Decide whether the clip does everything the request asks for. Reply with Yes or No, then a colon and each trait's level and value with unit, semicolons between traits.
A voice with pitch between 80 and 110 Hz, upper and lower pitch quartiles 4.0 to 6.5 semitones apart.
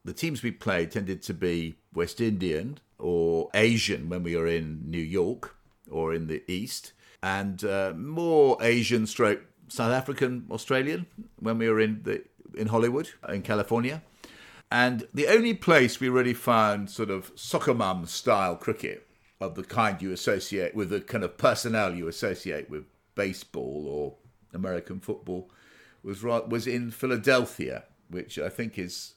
Yes: low, 105 Hz; average, 4.7 semitones